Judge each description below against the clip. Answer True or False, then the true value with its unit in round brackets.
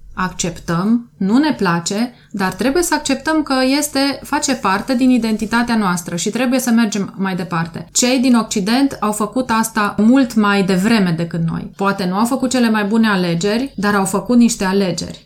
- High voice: True (220 Hz)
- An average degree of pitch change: True (4.6 semitones)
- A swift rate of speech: True (175 wpm)